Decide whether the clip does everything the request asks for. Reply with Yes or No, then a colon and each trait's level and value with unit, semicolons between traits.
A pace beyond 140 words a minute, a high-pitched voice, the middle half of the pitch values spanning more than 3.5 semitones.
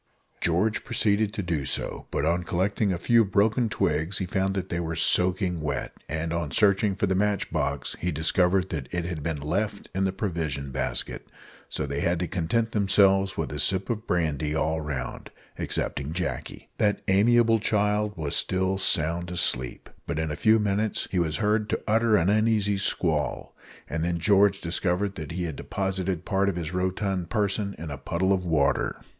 No: average, 185 wpm; very low, 95 Hz; average, 3.9 semitones